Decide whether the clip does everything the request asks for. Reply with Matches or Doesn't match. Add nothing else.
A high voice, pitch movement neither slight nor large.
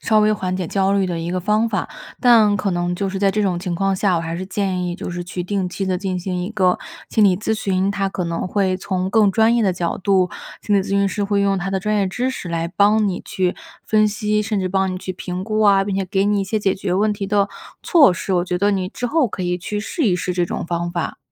Doesn't match